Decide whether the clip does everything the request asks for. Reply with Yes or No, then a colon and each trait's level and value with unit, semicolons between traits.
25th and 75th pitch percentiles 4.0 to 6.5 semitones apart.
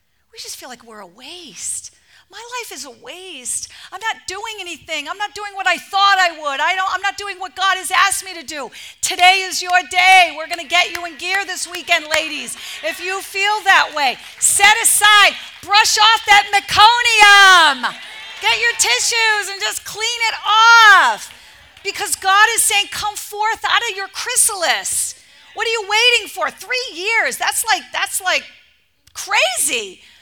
No: average, 3.1 semitones